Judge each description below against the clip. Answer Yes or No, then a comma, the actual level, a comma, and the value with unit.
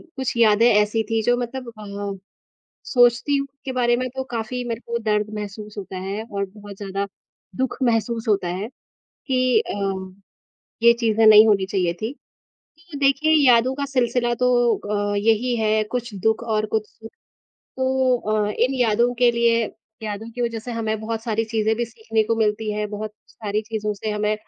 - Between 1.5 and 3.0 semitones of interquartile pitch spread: Yes, narrow, 2.4 semitones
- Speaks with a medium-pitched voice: No, high, 225 Hz